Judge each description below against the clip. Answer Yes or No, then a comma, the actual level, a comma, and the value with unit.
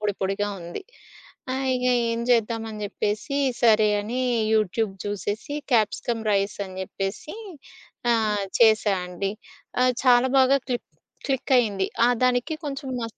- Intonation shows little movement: No, average, 3.5 semitones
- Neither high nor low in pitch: No, high, 225 Hz